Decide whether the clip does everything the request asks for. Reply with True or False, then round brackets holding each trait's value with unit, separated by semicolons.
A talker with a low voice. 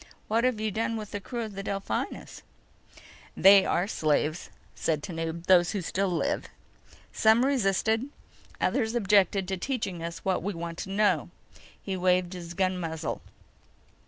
False (190 Hz)